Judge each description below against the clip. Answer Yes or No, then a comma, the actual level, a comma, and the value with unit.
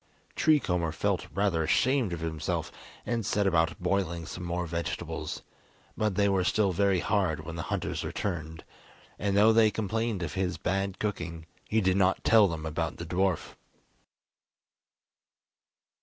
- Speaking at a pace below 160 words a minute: Yes, average, 150 wpm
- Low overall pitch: Yes, very low, 95 Hz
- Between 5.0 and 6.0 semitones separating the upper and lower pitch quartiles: No, average, 3.6 semitones